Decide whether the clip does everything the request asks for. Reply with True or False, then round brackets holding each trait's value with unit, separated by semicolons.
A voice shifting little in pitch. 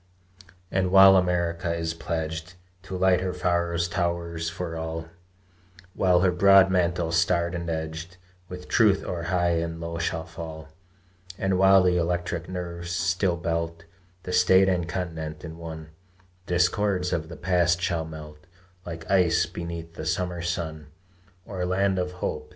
True (1.7 semitones)